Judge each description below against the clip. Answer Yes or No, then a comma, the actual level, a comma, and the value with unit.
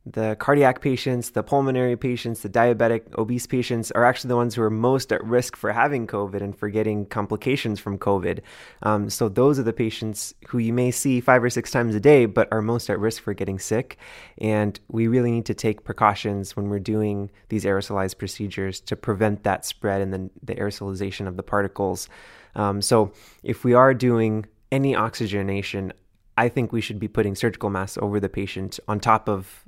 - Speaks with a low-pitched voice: Yes, low, 110 Hz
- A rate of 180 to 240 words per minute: Yes, average, 200 wpm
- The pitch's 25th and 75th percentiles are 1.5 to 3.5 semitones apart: Yes, average, 3.0 semitones